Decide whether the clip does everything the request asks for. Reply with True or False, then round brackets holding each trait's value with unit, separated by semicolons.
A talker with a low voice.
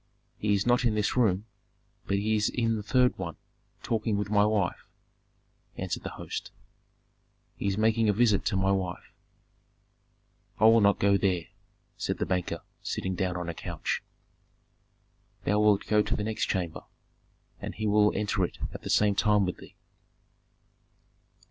True (105 Hz)